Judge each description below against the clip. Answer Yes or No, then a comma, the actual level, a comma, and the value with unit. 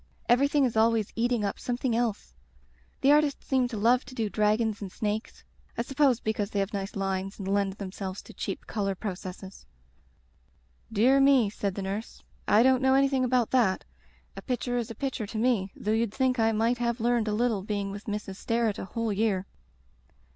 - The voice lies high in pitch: Yes, high, 225 Hz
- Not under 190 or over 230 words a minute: Yes, average, 195 wpm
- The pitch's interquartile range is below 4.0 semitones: Yes, average, 3.4 semitones